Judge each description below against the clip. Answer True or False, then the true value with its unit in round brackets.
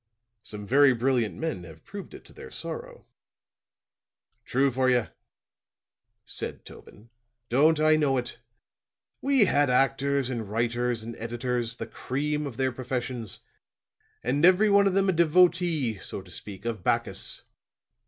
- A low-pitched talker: True (130 Hz)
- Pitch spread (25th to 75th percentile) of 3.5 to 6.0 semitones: True (4.8 semitones)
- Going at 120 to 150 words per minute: True (145 wpm)